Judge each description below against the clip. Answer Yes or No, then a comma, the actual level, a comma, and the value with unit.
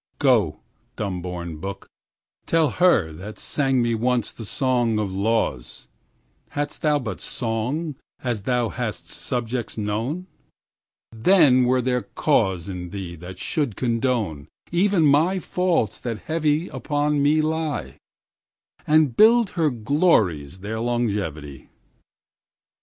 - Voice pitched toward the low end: Yes, low, 120 Hz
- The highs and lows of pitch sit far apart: Yes, wide, 6.7 semitones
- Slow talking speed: Yes, slow, 105 wpm